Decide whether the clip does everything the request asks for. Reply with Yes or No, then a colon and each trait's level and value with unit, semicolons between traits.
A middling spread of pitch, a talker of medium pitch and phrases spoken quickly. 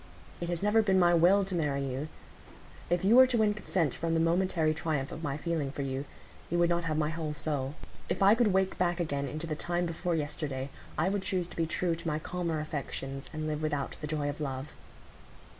Yes: average, 3.0 semitones; medium, 165 Hz; fast, 225 wpm